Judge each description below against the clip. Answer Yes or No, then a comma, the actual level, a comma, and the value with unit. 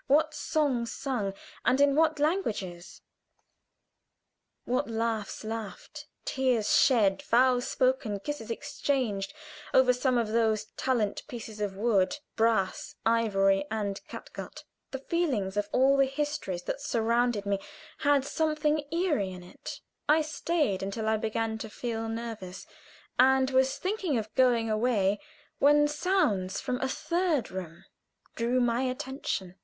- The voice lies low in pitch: No, high, 235 Hz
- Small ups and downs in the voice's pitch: No, average, 4.7 semitones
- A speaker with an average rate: No, slow, 130 wpm